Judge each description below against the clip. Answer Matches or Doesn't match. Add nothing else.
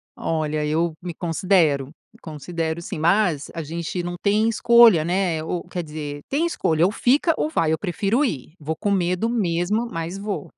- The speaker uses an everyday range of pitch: Matches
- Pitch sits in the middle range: Matches